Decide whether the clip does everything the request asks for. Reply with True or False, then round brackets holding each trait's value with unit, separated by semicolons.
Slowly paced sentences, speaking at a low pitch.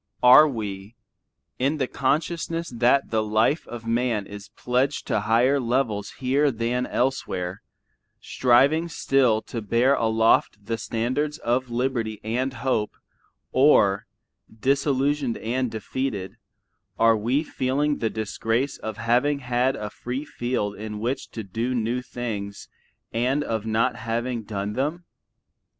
True (130 wpm; 120 Hz)